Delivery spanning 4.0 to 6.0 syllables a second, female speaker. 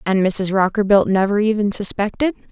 Yes: 5.3 syllables/s; female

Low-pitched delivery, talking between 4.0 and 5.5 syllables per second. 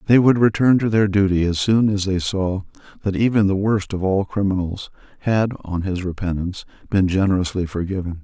Yes: very low, 95 Hz; 5.4 syllables/s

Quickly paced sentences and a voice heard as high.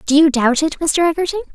Yes: fast, 230 wpm; very high, 310 Hz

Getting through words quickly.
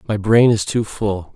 Yes: fast, 220 wpm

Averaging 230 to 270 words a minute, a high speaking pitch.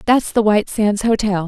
No: fast, 205 wpm; high, 210 Hz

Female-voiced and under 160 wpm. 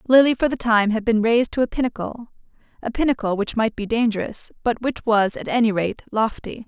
No: female; average, 200 wpm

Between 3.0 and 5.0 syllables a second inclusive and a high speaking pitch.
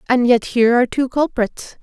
No: 5.5 syllables/s; high, 245 Hz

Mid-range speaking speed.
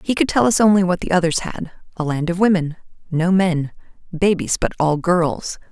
Yes: average, 170 wpm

